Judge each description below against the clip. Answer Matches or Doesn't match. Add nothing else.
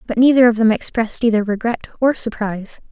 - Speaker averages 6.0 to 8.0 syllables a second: Matches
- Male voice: Doesn't match